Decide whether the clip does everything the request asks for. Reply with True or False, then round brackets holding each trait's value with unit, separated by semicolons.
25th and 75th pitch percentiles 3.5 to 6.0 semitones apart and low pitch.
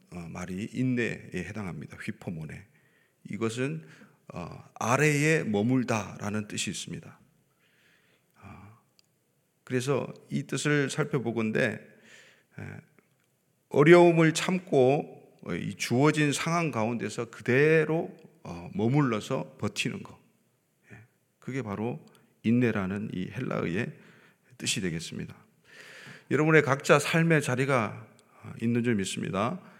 True (5.1 semitones; 130 Hz)